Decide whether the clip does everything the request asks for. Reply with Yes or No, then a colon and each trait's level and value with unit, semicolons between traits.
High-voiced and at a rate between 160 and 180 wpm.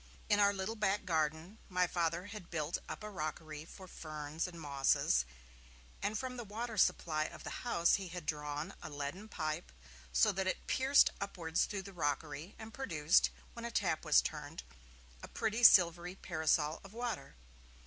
No: medium, 175 Hz; average, 170 wpm